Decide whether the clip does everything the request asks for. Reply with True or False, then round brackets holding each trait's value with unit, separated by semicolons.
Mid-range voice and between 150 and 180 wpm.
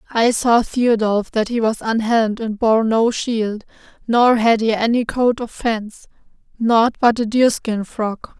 False (225 Hz; 170 wpm)